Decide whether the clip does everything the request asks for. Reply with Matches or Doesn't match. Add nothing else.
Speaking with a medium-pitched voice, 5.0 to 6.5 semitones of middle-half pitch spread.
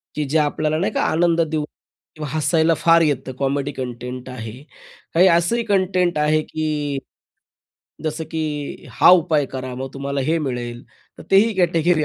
Doesn't match